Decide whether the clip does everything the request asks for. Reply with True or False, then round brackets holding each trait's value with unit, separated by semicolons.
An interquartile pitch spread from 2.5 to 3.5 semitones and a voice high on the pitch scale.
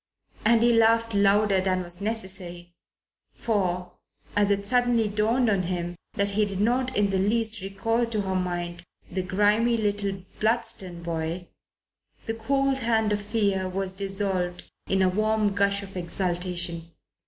True (3.2 semitones; 200 Hz)